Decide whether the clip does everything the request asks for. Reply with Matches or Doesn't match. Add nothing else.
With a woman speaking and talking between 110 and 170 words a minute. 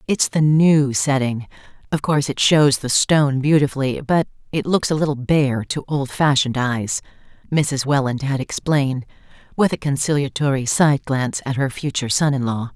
Matches